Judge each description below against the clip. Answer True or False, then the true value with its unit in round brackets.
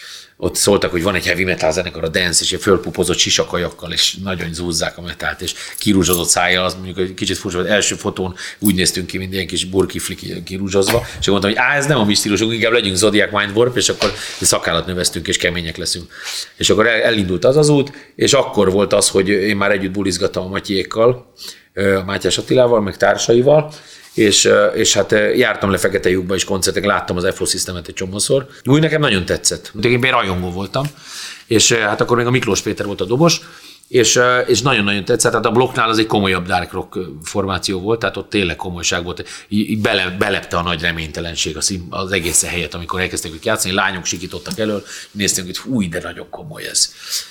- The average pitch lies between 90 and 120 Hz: True (95 Hz)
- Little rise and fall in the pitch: False (3.6 semitones)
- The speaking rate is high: True (195 wpm)